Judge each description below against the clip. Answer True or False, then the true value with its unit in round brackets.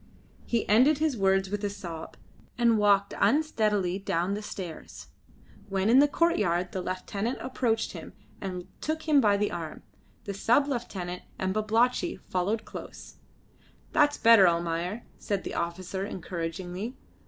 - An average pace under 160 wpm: True (140 wpm)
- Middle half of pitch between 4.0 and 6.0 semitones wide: True (4.3 semitones)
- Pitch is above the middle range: True (200 Hz)